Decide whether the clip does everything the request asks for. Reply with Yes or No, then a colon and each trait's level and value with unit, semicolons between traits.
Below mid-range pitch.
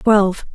No: high, 200 Hz